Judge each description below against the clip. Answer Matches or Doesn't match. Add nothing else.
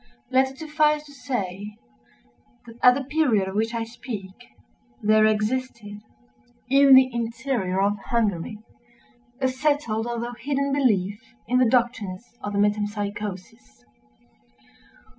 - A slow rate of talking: Matches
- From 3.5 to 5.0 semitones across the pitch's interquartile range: Matches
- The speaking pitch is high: Matches